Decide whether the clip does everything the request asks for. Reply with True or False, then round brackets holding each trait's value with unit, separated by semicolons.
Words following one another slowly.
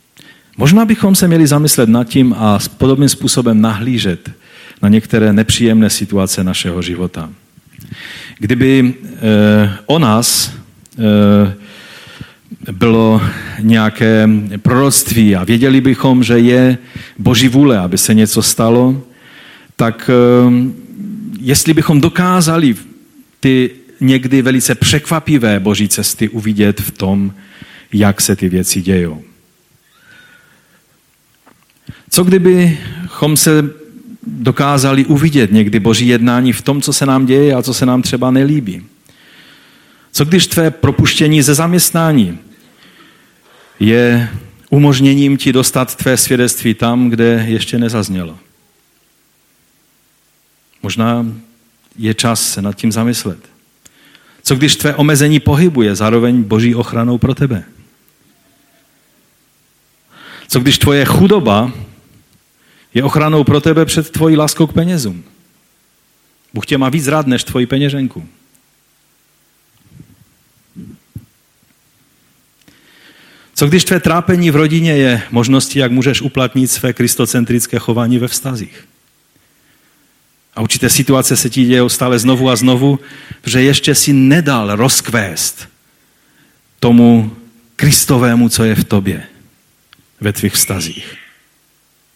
True (110 wpm)